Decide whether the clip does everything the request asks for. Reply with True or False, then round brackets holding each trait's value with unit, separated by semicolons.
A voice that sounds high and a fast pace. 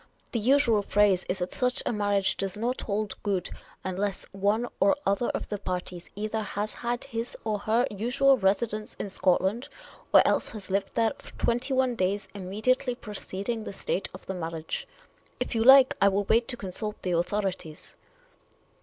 False (205 Hz; 180 wpm)